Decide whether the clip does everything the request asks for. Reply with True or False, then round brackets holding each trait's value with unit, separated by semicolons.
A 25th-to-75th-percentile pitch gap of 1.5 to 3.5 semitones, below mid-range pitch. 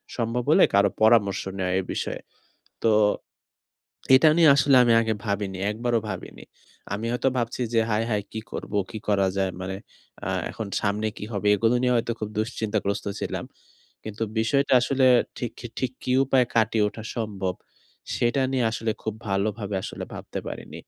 True (2.9 semitones; 110 Hz)